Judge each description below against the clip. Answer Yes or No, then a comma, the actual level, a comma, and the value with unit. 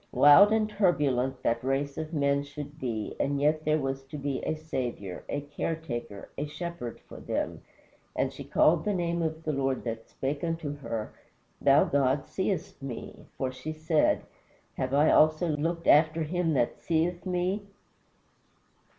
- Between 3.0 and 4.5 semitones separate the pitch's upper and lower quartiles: Yes, average, 3.4 semitones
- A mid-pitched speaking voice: Yes, medium, 150 Hz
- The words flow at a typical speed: Yes, average, 170 wpm